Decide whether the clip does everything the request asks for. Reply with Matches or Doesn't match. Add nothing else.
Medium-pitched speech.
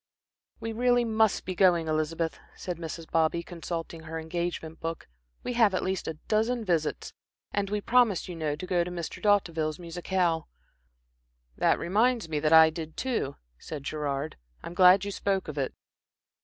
Matches